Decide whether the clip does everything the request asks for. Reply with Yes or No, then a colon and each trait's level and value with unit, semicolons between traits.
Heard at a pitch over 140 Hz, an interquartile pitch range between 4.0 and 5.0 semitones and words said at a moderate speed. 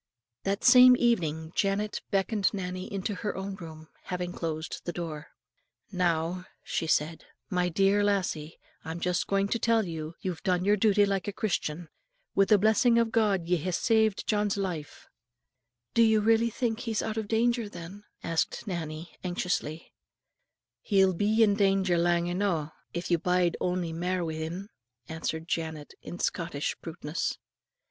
No: medium, 185 Hz; average, 3.6 semitones; average, 160 wpm